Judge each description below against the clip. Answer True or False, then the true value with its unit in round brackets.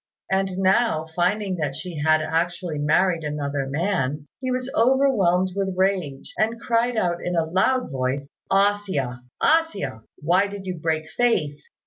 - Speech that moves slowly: False (155 wpm)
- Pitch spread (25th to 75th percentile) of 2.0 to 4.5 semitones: False (5.0 semitones)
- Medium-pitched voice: True (180 Hz)